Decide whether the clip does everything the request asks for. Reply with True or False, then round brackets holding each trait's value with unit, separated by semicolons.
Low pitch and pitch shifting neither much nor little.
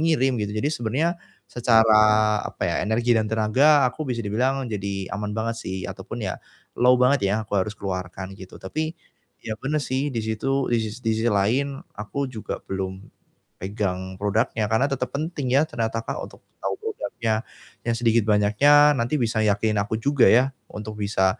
True (110 Hz; 4.1 semitones)